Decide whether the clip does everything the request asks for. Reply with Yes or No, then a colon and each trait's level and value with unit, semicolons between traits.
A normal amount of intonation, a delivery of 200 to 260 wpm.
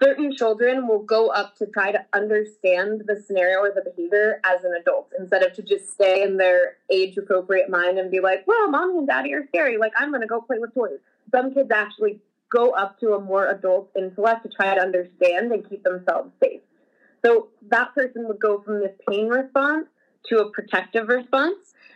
Yes: average, 4.3 semitones; fast, 205 wpm